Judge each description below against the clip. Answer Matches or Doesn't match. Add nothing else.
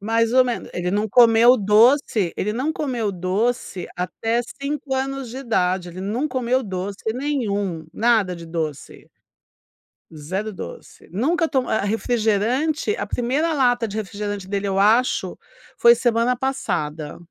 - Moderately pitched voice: Doesn't match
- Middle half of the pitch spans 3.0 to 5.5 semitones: Matches